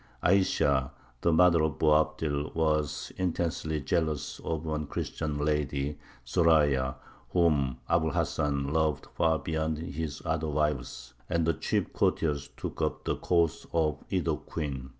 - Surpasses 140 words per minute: No, slow, 135 wpm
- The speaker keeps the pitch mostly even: Yes, narrow, 2.1 semitones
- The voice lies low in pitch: Yes, very low, 75 Hz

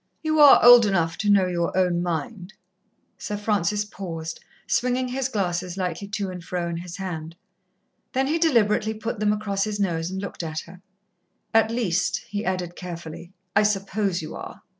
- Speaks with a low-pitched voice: No, high, 195 Hz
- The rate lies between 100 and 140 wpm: No, average, 175 wpm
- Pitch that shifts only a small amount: No, average, 3.6 semitones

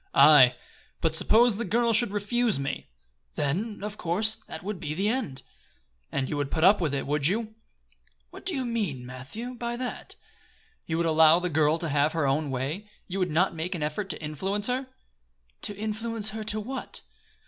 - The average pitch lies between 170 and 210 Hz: Yes, medium, 185 Hz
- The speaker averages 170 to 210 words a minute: Yes, average, 190 wpm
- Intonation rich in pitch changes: Yes, wide, 6.4 semitones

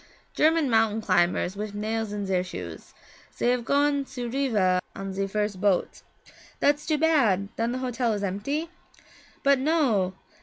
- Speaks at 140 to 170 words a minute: Yes, average, 155 wpm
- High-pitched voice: Yes, high, 225 Hz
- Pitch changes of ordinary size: No, wide, 5.9 semitones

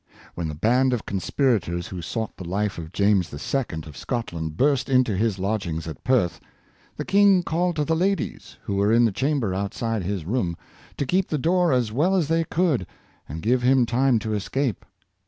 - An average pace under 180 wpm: No, average, 190 wpm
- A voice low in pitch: Yes, low, 115 Hz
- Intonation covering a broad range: Yes, wide, 6.8 semitones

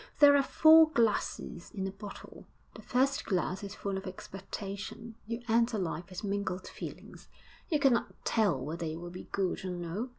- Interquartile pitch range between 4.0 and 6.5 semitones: Yes, average, 4.3 semitones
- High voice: Yes, high, 200 Hz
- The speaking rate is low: No, average, 175 wpm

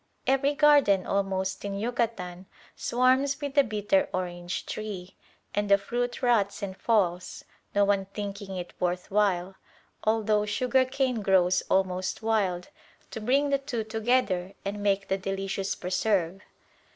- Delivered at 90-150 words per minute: Yes, average, 140 wpm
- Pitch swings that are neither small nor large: Yes, average, 4.2 semitones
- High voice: Yes, high, 205 Hz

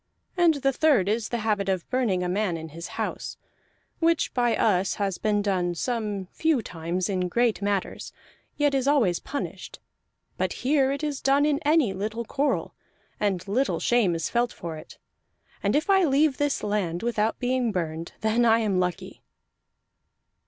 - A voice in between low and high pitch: No, high, 220 Hz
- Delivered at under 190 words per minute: Yes, average, 170 wpm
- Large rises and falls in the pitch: Yes, wide, 6.3 semitones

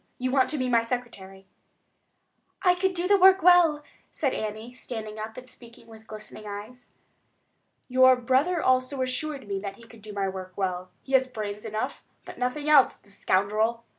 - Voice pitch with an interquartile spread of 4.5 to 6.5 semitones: No, average, 3.9 semitones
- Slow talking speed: No, average, 180 wpm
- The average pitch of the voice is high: Yes, high, 245 Hz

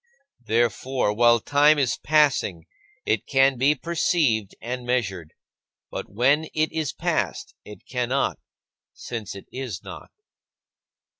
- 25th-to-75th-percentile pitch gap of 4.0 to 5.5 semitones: Yes, average, 4.6 semitones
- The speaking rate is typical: No, slow, 120 wpm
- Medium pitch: No, low, 125 Hz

